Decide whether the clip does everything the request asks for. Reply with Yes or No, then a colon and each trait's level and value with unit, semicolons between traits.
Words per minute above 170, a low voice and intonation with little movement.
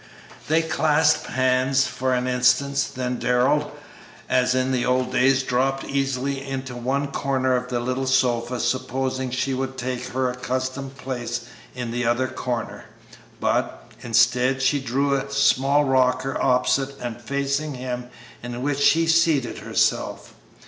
No: average, 140 wpm; low, 130 Hz; narrow, 1.5 semitones